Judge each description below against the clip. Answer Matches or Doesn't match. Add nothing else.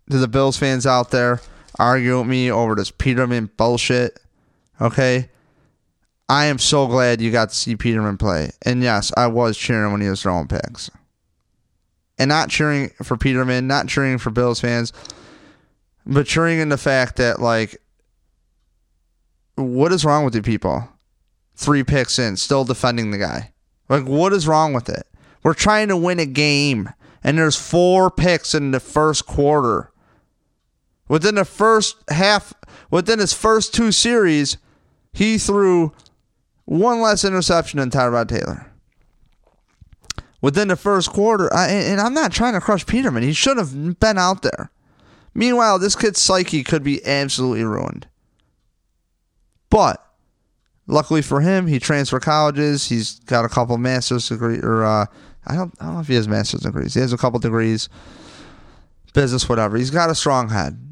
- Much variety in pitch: Matches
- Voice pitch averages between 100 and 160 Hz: Matches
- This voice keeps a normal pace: Matches